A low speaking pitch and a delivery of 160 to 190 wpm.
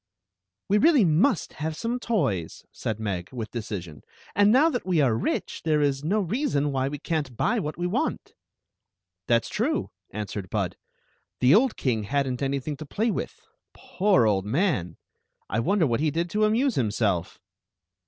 No: medium, 145 Hz; average, 180 wpm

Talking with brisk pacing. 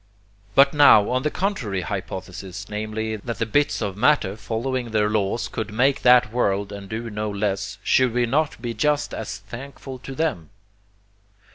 No: average, 165 wpm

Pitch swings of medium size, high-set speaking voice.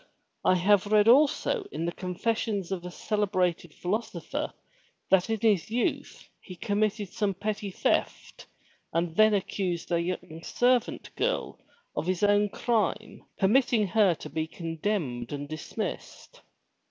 Yes: average, 3.7 semitones; high, 200 Hz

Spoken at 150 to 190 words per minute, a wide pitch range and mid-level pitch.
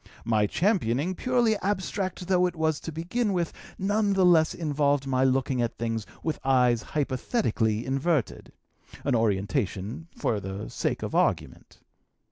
No: average, 140 wpm; wide, 7.6 semitones; medium, 145 Hz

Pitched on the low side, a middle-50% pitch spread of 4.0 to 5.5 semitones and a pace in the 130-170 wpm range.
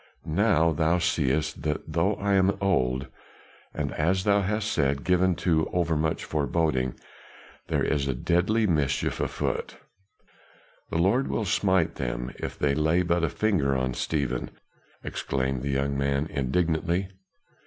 Yes: very low, 80 Hz; average, 5.0 semitones; average, 145 wpm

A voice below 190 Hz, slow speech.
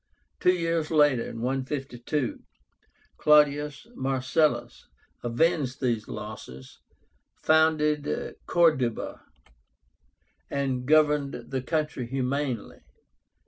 Yes: medium, 140 Hz; slow, 70 wpm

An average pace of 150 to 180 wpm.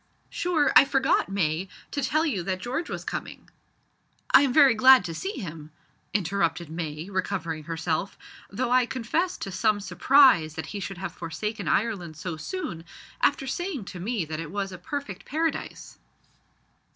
Yes: average, 165 wpm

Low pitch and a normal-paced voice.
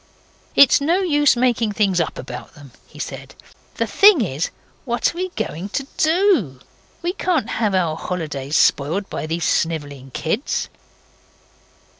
No: high, 205 Hz; average, 145 wpm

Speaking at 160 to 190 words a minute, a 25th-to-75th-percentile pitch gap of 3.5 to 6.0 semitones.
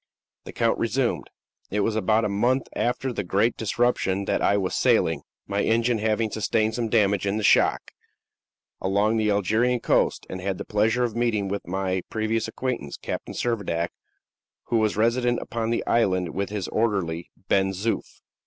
No: average, 170 wpm; average, 2.8 semitones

